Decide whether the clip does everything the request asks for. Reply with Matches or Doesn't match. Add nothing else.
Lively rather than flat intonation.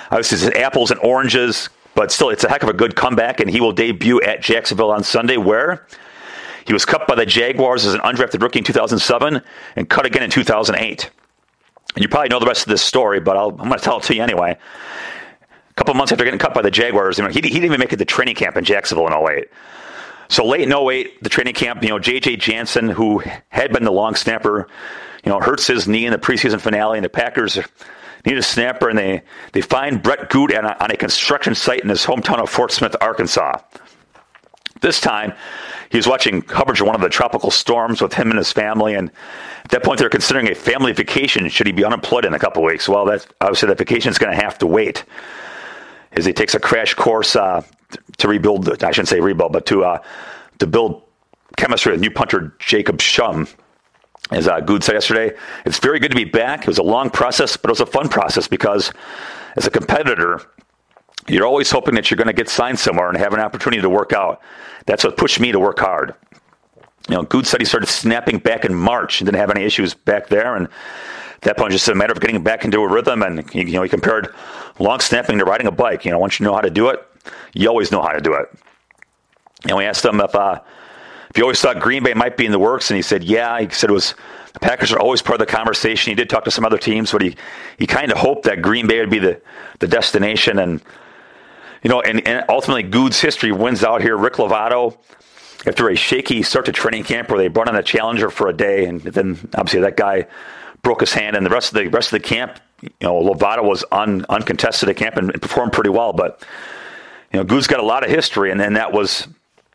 Doesn't match